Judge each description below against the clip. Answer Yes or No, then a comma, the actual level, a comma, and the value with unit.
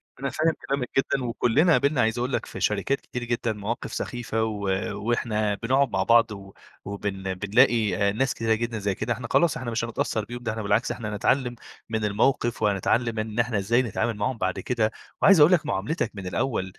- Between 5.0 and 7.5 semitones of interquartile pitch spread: No, average, 3.1 semitones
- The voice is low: Yes, low, 115 Hz